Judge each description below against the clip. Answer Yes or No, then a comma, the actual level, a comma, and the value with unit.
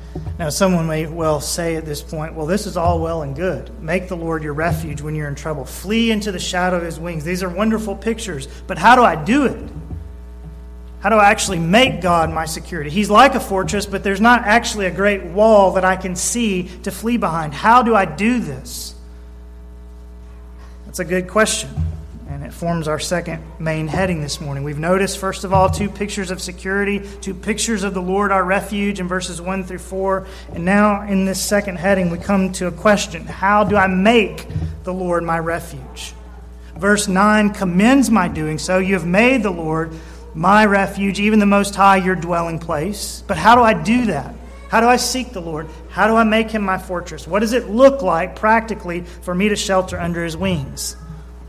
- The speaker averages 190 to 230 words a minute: Yes, fast, 205 wpm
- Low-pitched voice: No, medium, 185 Hz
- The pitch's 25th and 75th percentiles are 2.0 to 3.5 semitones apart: No, average, 4.1 semitones